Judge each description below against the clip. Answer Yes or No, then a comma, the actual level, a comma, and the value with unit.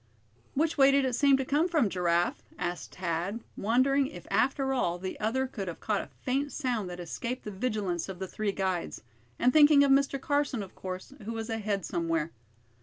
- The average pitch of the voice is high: Yes, high, 225 Hz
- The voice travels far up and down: Yes, wide, 6.6 semitones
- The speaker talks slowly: No, average, 195 wpm